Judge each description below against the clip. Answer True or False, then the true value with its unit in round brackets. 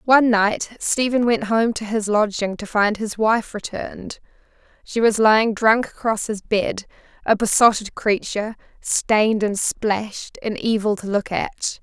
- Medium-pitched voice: False (215 Hz)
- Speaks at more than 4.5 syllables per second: False (4.4 syllables/s)